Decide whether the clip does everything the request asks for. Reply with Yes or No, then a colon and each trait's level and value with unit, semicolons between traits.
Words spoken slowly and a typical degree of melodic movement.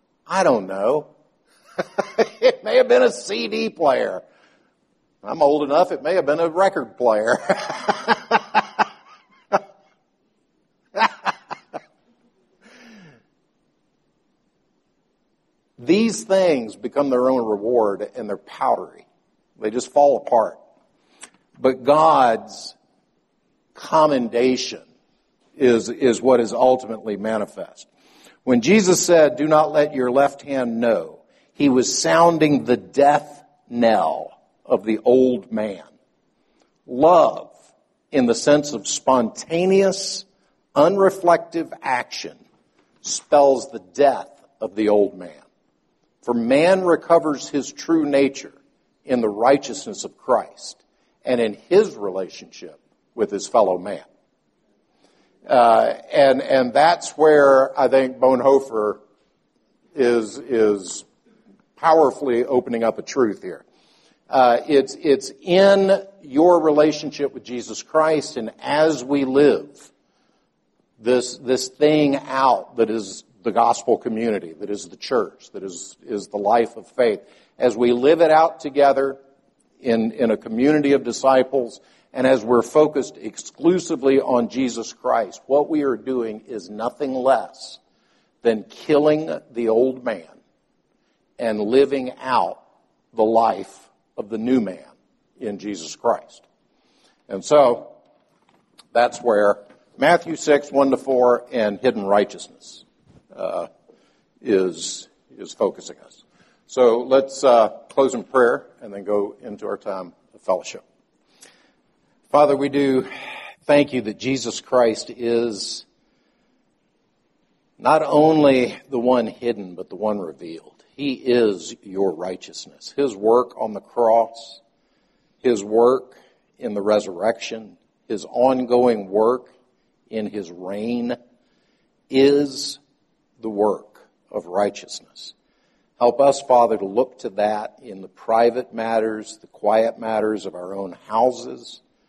Yes: slow, 120 wpm; average, 4.3 semitones